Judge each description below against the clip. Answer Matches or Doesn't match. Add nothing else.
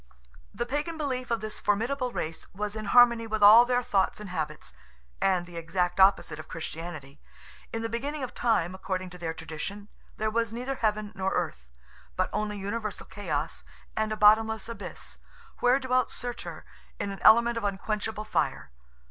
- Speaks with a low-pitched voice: Doesn't match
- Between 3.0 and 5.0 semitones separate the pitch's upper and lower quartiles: Matches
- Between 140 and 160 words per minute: Doesn't match